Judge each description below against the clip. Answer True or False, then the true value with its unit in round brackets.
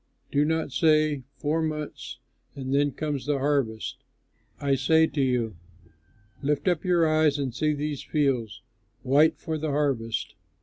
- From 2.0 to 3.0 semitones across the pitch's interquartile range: True (2.4 semitones)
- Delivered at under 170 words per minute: True (145 wpm)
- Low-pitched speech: False (145 Hz)